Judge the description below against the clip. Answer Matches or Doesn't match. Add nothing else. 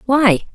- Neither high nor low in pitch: Doesn't match